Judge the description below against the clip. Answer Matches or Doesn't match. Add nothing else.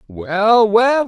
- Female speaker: Doesn't match